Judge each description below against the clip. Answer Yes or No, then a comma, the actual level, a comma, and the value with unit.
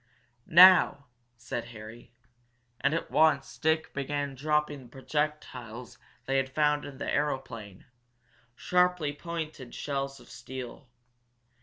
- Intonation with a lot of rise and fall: No, average, 3.2 semitones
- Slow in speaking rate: Yes, slow, 110 wpm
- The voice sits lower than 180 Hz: Yes, medium, 140 Hz